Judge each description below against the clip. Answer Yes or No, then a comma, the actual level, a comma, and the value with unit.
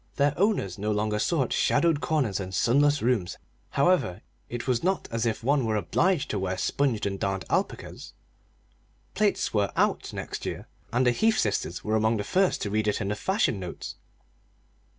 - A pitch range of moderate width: No, wide, 6.0 semitones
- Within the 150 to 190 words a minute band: Yes, average, 180 wpm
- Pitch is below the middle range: Yes, low, 115 Hz